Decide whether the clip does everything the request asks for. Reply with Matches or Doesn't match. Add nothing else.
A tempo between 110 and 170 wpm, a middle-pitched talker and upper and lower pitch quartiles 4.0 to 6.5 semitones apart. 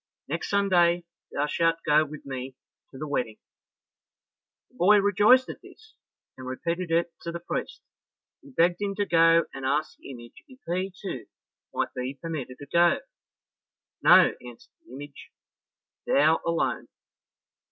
Matches